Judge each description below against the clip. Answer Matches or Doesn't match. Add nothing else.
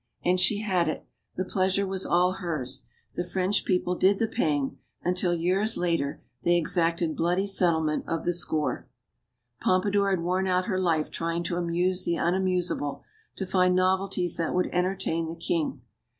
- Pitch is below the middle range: Doesn't match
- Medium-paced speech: Matches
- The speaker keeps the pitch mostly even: Matches